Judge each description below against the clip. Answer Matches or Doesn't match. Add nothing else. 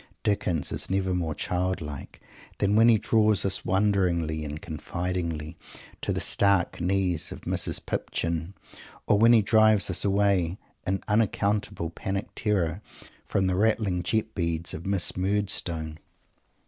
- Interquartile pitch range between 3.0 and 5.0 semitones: Matches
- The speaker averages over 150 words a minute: Doesn't match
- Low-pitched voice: Matches